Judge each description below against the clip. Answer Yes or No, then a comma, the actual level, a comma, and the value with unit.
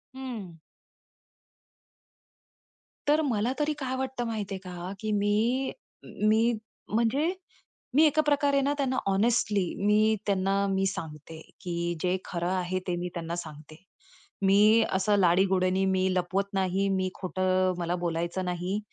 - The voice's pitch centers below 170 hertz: No, high, 195 Hz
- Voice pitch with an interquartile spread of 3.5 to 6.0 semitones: Yes, average, 4.0 semitones